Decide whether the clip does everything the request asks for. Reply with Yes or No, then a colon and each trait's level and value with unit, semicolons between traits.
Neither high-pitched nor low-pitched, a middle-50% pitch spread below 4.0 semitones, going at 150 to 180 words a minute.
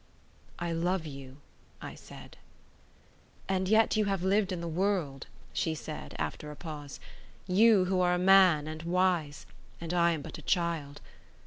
Yes: medium, 175 Hz; average, 3.3 semitones; average, 155 wpm